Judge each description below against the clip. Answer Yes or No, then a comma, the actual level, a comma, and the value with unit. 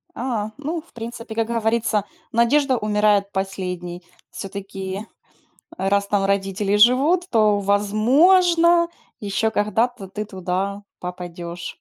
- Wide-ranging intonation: No, average, 3.3 semitones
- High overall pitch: Yes, high, 210 Hz